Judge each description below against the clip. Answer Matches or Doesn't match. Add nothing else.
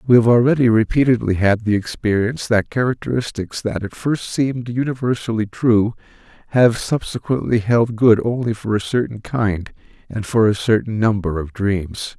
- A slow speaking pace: Doesn't match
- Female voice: Doesn't match